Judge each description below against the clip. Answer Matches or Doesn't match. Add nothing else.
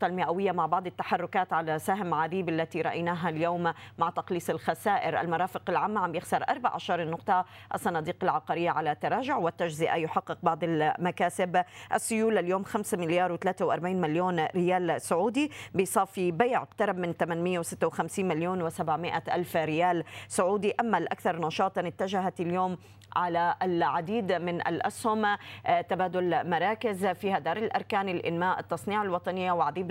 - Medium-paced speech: Matches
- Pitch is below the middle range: Doesn't match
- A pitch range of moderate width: Doesn't match